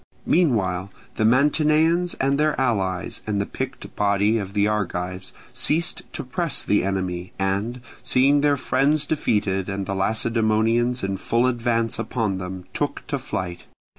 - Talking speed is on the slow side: No, average, 145 wpm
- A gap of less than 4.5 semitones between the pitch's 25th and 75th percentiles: No, average, 5.3 semitones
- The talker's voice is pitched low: Yes, low, 110 Hz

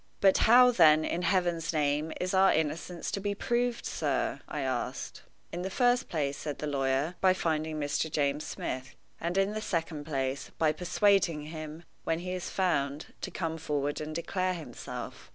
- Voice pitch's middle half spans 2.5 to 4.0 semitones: Yes, average, 3.7 semitones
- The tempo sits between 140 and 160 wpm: No, average, 175 wpm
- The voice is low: No, medium, 165 Hz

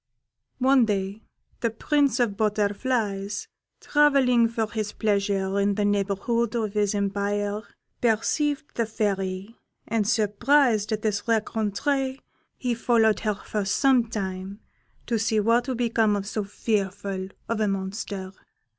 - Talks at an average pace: No, slow, 130 wpm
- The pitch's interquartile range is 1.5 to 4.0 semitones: Yes, average, 2.7 semitones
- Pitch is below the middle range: No, high, 215 Hz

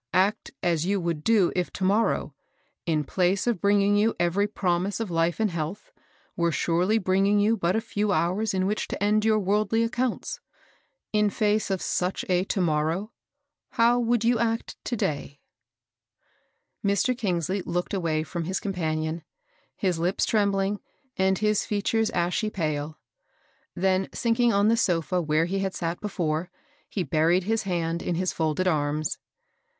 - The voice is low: No, high, 190 Hz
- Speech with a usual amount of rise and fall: Yes, average, 3.7 semitones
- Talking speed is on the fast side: No, average, 165 wpm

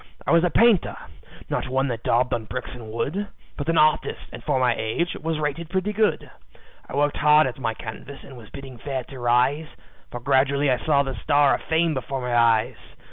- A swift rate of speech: Yes, fast, 210 wpm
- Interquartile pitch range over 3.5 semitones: Yes, average, 3.9 semitones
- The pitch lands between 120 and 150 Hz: Yes, low, 135 Hz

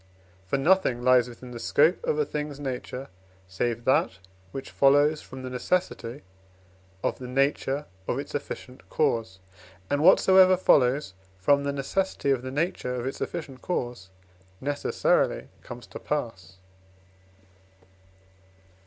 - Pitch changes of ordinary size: Yes, average, 3.2 semitones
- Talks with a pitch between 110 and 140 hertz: Yes, low, 135 Hz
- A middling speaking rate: No, slow, 130 wpm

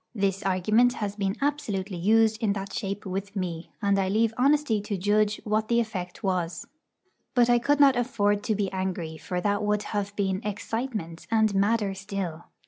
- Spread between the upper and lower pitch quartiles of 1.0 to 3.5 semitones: Yes, narrow, 2.5 semitones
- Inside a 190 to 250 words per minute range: No, average, 180 wpm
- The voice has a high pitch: Yes, high, 205 Hz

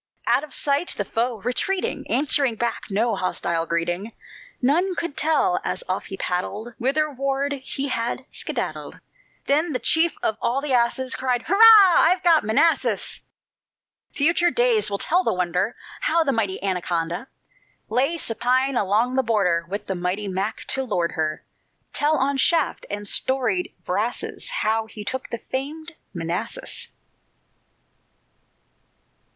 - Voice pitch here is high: Yes, very high, 250 Hz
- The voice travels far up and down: Yes, wide, 6.8 semitones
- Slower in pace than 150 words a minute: Yes, average, 140 wpm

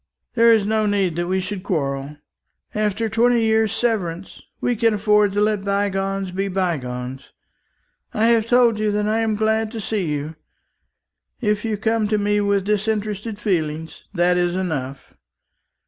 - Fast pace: No, average, 160 wpm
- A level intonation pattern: No, average, 3.3 semitones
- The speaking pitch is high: Yes, high, 205 Hz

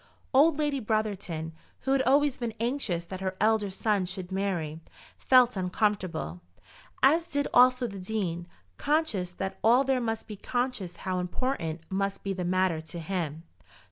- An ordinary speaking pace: Yes, average, 155 wpm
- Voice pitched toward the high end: Yes, high, 200 Hz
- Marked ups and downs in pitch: Yes, wide, 5.7 semitones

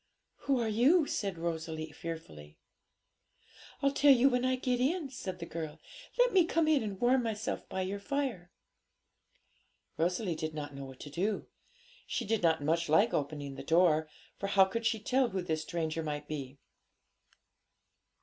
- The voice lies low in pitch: No, medium, 185 Hz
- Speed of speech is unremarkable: Yes, average, 165 wpm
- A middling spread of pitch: No, wide, 7.7 semitones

